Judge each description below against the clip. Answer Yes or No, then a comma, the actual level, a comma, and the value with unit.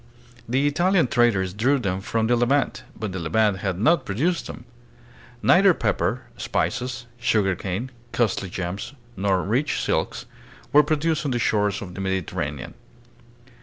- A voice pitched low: Yes, low, 110 Hz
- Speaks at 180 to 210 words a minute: No, average, 145 wpm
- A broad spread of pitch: Yes, wide, 5.9 semitones